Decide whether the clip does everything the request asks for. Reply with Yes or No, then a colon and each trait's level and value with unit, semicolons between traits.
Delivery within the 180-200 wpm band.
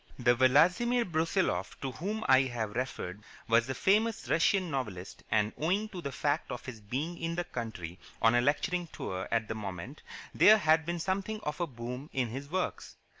Yes: average, 185 wpm